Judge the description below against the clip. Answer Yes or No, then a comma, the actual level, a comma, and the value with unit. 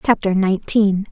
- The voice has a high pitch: Yes, high, 195 Hz